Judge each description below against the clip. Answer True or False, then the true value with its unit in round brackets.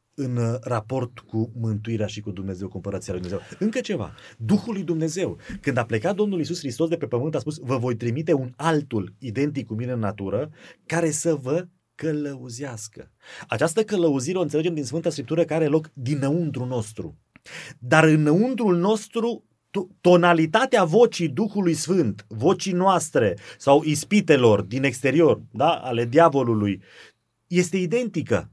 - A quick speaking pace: False (145 wpm)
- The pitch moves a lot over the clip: True (6.4 semitones)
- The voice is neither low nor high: True (150 Hz)